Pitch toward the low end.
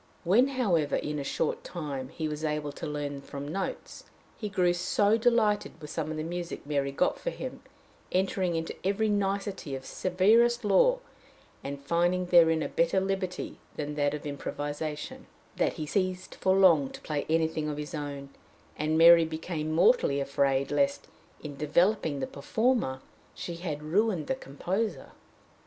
No: medium, 165 Hz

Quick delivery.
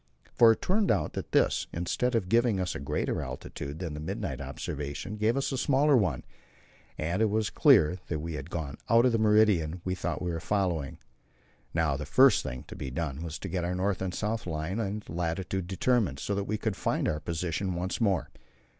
Yes: fast, 215 wpm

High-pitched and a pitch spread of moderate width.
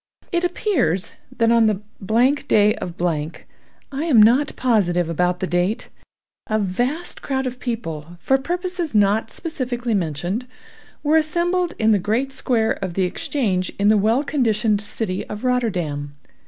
No: high, 220 Hz; wide, 6.2 semitones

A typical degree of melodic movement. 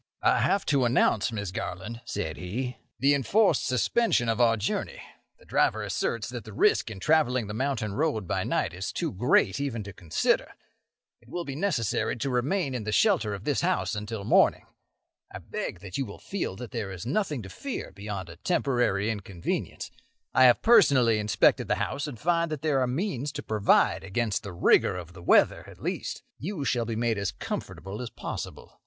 No: wide, 5.7 semitones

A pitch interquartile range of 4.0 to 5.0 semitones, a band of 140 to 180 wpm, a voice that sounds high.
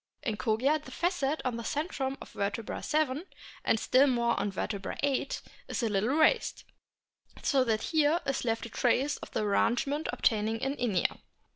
Yes: average, 4.5 semitones; average, 170 wpm; very high, 255 Hz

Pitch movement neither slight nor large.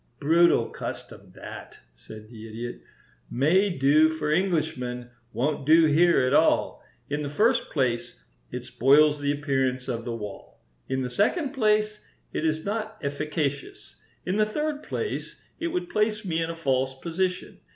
No: wide, 6.5 semitones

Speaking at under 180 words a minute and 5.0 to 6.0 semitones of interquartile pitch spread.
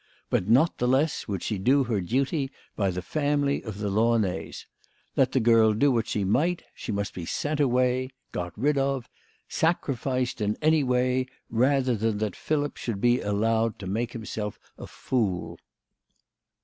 No: average, 165 wpm; average, 4.5 semitones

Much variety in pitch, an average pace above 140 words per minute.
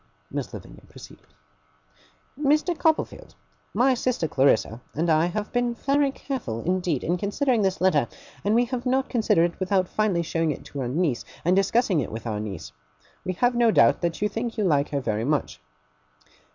Yes: wide, 8.1 semitones; average, 180 wpm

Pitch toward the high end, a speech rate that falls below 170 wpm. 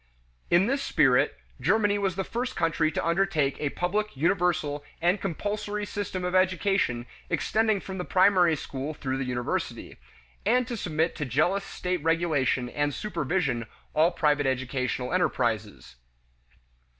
No: medium, 170 Hz; average, 140 wpm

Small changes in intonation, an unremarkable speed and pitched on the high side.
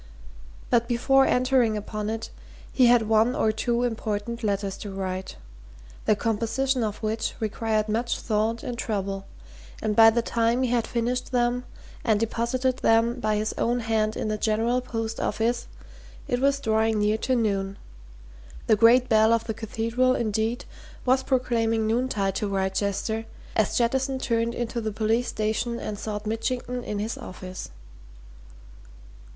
Yes: narrow, 2.1 semitones; average, 150 wpm; high, 225 Hz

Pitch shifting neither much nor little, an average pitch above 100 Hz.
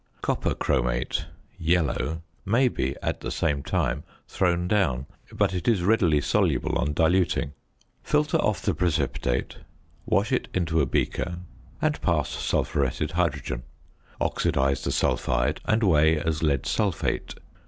No: average, 4.7 semitones; very low, 80 Hz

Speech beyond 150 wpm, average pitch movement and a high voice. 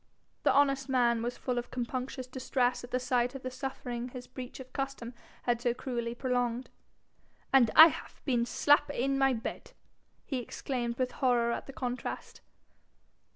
No: average, 165 wpm; narrow, 1.7 semitones; very high, 250 Hz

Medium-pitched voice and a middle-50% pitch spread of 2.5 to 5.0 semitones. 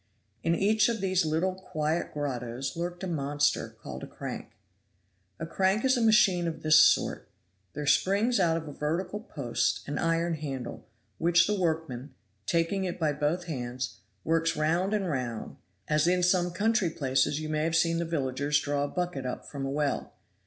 Yes: medium, 165 Hz; average, 3.7 semitones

